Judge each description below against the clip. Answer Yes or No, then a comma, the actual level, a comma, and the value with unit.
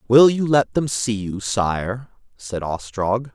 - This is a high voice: No, low, 115 Hz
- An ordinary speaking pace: Yes, average, 160 wpm